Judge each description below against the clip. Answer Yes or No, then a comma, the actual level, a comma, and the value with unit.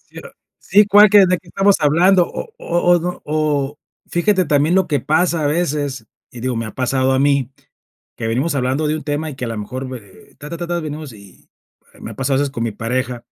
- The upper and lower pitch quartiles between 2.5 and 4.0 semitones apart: No, average, 4.9 semitones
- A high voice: No, medium, 145 Hz